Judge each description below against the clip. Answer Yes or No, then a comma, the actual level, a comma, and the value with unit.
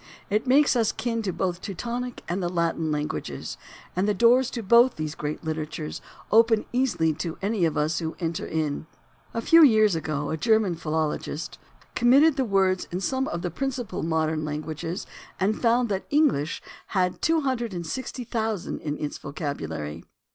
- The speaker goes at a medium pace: Yes, average, 175 wpm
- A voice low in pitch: No, medium, 185 Hz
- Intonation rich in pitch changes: Yes, wide, 6.8 semitones